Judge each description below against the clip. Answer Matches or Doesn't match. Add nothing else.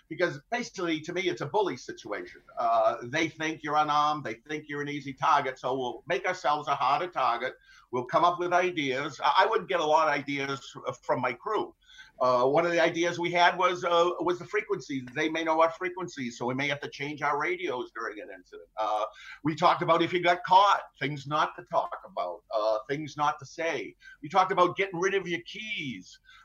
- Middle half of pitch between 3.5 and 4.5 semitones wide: Matches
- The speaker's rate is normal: Doesn't match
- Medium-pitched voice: Matches